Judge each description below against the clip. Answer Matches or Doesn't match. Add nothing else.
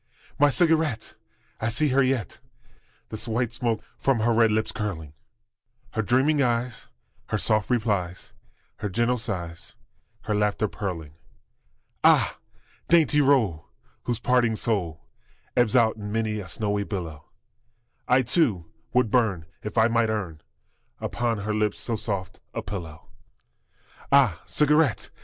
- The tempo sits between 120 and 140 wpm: Matches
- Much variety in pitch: Doesn't match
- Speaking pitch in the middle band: Doesn't match